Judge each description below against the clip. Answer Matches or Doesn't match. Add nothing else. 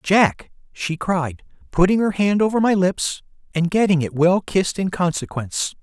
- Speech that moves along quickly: Doesn't match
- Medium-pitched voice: Matches